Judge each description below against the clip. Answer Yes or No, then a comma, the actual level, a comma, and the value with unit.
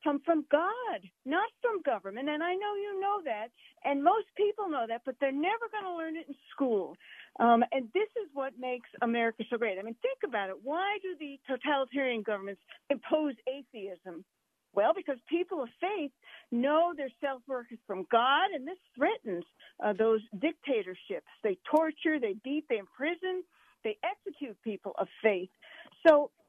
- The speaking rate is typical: Yes, average, 170 wpm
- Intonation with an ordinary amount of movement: No, wide, 6.8 semitones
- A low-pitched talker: No, very high, 285 Hz